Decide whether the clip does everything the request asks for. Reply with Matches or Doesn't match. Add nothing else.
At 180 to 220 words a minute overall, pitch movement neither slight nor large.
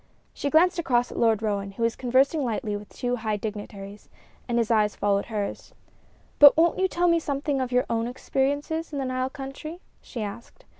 Matches